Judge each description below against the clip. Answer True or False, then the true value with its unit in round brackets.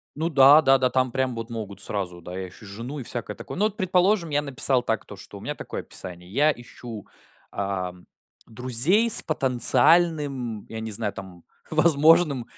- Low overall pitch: True (125 Hz)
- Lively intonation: True (6.3 semitones)